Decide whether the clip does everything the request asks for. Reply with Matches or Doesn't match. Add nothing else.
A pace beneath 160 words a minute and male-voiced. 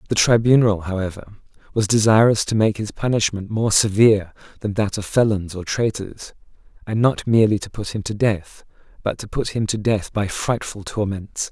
Doesn't match